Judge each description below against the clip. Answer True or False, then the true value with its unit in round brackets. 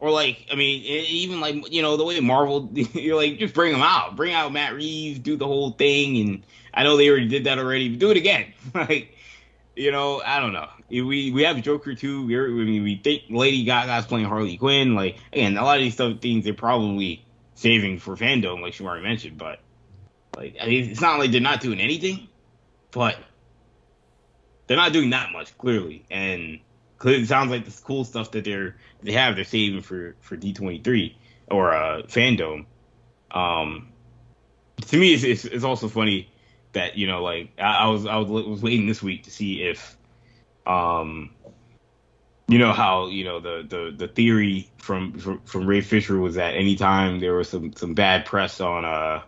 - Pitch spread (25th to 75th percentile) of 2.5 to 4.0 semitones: False (5.5 semitones)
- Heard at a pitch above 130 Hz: False (115 Hz)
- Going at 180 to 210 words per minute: True (200 wpm)